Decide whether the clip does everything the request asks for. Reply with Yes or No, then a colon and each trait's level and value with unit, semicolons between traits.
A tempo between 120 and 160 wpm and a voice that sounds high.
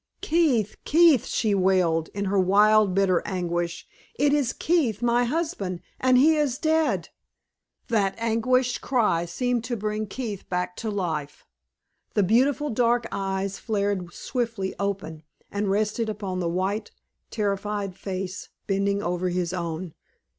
Yes: slow, 135 wpm; high, 205 Hz